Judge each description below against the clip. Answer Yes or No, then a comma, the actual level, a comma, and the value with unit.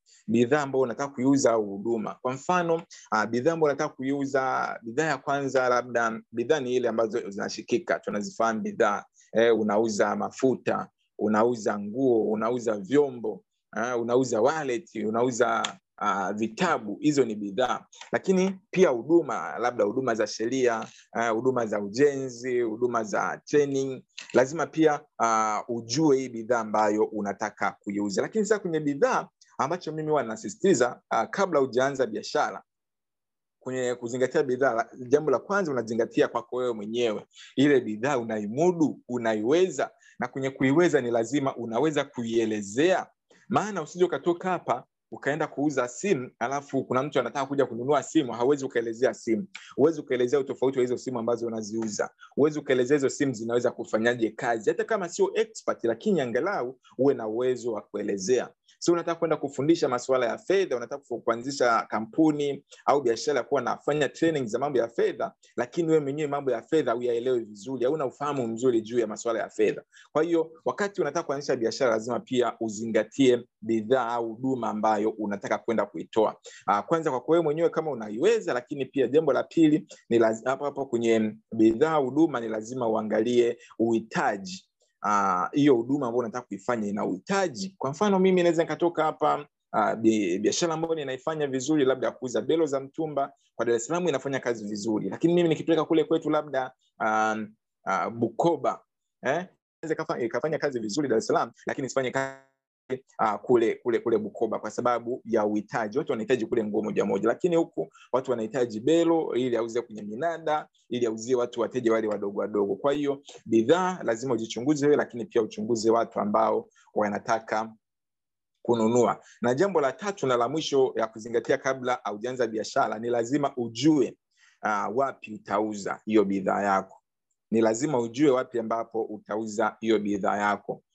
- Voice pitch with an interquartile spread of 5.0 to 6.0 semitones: Yes, average, 5.3 semitones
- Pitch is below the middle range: Yes, low, 125 Hz